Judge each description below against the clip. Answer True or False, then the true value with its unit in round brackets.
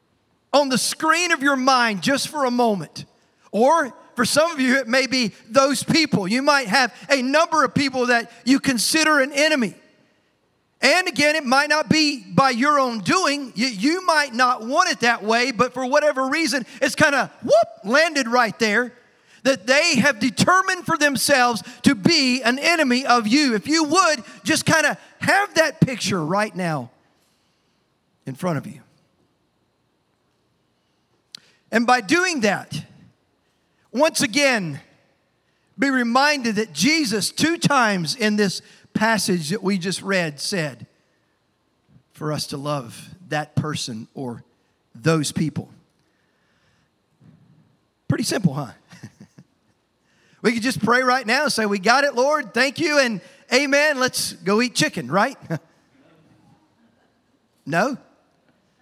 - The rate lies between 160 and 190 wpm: False (145 wpm)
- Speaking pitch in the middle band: False (250 Hz)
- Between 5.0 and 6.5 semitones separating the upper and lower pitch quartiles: True (5.6 semitones)